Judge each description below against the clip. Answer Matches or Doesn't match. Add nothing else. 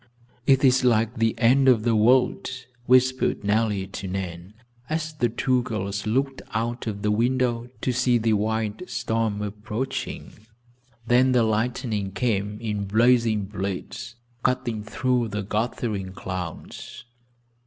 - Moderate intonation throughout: Matches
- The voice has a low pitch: Matches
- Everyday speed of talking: Doesn't match